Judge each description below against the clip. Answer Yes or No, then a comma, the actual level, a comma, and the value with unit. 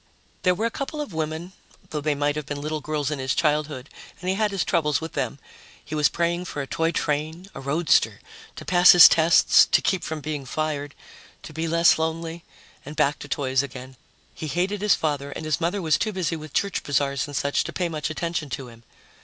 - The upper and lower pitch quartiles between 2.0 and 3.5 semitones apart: Yes, average, 2.9 semitones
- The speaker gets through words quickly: Yes, fast, 220 wpm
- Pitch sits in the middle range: Yes, medium, 155 Hz